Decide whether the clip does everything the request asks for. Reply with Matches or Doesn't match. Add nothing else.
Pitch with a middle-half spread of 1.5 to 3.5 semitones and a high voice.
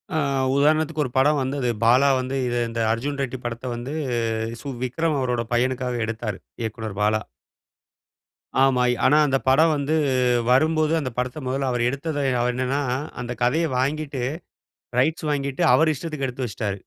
Doesn't match